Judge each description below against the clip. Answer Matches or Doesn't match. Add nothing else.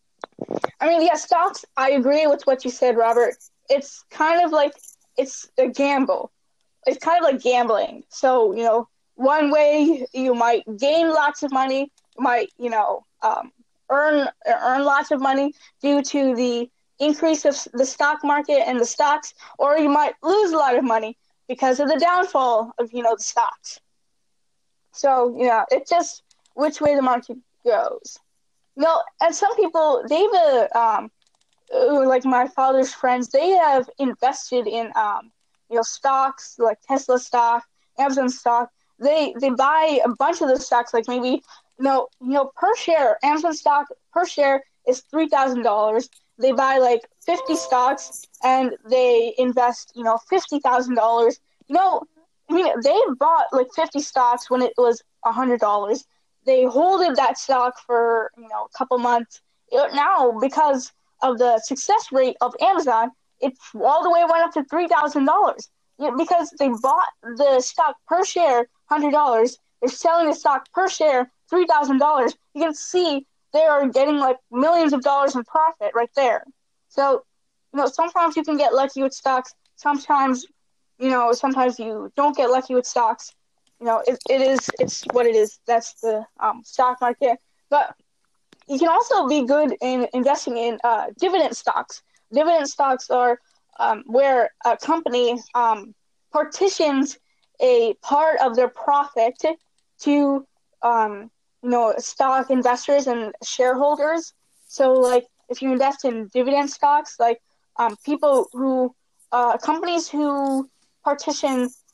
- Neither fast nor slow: Matches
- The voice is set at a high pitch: Matches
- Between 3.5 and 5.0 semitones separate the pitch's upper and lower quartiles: Matches